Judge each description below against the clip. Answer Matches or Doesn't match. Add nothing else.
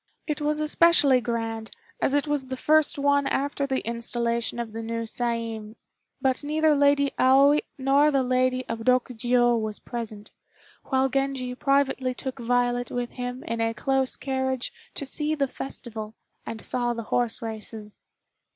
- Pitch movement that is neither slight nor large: Matches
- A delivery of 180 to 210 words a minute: Doesn't match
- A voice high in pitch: Matches